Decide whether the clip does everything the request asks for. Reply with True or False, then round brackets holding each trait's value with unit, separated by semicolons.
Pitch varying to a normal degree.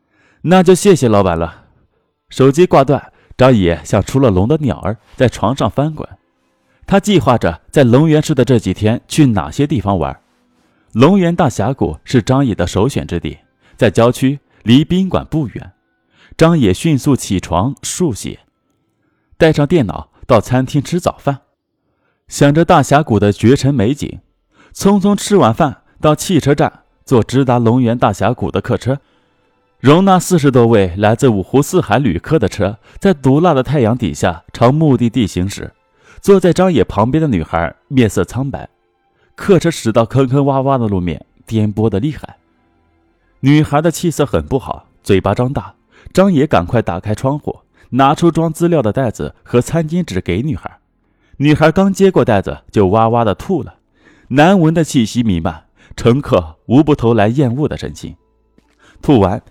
False (7.2 semitones)